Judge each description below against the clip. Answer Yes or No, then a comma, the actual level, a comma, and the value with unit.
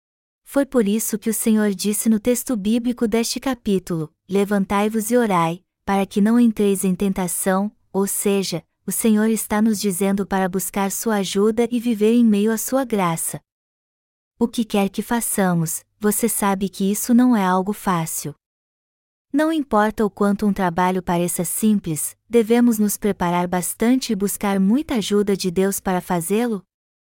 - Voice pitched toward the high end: Yes, high, 205 Hz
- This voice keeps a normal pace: Yes, average, 160 wpm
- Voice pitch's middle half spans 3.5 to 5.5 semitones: No, average, 2.8 semitones